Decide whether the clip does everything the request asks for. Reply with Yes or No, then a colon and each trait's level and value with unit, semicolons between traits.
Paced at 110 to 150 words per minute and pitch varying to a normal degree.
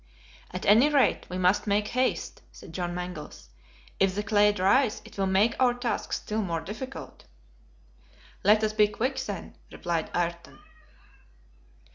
Yes: average, 145 wpm; average, 3.6 semitones